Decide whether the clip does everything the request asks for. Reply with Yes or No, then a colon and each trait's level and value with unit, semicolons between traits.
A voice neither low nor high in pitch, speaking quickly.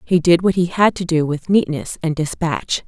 Yes: medium, 170 Hz; fast, 230 wpm